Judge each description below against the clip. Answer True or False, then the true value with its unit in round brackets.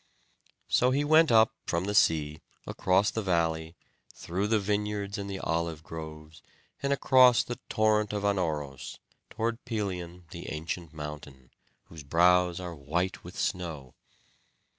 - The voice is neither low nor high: False (90 Hz)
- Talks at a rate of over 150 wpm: False (140 wpm)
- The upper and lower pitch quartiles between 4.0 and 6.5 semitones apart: True (4.6 semitones)